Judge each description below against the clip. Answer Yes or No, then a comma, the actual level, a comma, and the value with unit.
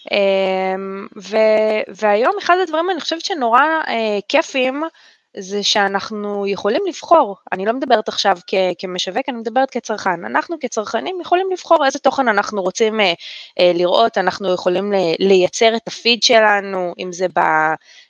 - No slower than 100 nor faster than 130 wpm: No, average, 145 wpm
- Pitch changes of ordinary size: No, wide, 6.1 semitones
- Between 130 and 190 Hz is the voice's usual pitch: No, high, 210 Hz